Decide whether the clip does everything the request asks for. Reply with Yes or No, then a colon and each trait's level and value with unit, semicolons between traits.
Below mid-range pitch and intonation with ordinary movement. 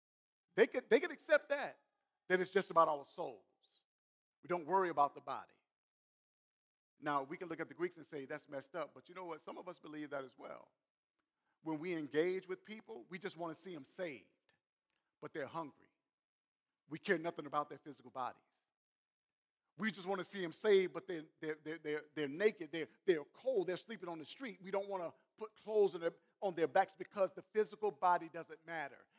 No: medium, 175 Hz; average, 4.0 semitones